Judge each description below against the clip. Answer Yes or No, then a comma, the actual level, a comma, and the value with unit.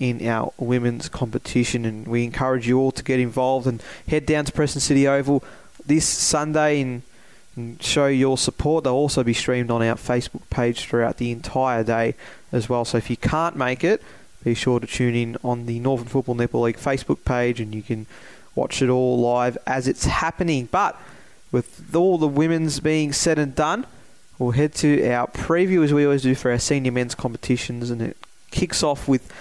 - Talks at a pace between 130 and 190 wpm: No, average, 200 wpm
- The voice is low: Yes, low, 125 Hz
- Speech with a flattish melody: No, average, 3.1 semitones